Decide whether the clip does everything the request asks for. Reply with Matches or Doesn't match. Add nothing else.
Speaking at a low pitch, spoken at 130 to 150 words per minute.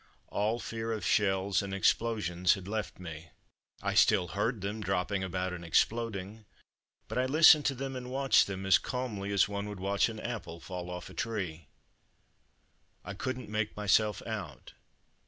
Doesn't match